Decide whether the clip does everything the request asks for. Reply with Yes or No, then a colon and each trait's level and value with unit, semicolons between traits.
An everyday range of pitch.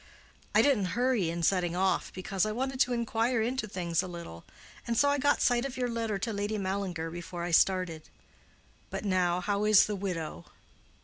Yes: average, 4.8 semitones